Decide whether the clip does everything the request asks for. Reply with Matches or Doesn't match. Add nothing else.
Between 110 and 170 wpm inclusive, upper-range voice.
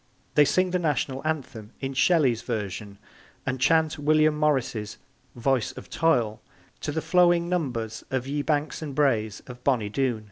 Doesn't match